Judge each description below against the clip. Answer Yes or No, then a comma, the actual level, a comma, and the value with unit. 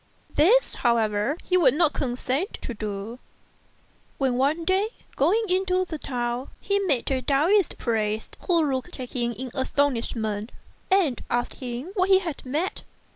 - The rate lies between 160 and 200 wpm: No, average, 150 wpm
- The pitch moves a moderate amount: No, wide, 7.0 semitones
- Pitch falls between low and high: No, very high, 270 Hz